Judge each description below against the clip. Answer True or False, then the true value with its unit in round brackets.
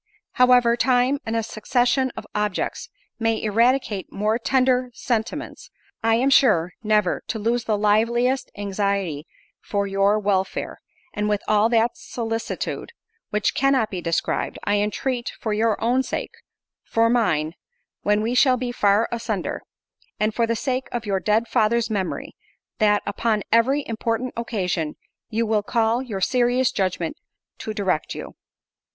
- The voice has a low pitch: False (225 Hz)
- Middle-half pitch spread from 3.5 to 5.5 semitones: False (2.8 semitones)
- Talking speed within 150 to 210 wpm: False (140 wpm)